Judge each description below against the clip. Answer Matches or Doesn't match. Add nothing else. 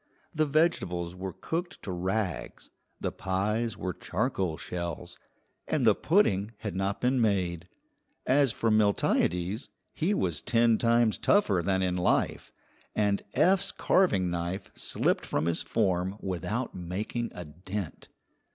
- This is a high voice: Doesn't match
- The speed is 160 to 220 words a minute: Doesn't match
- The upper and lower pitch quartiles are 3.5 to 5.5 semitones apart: Matches